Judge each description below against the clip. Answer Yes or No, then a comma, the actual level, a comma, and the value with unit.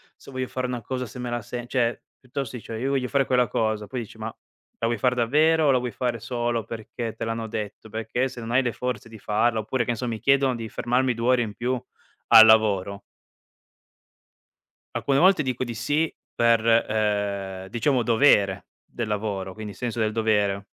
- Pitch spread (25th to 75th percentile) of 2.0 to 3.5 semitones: Yes, narrow, 2.5 semitones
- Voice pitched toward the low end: Yes, low, 115 Hz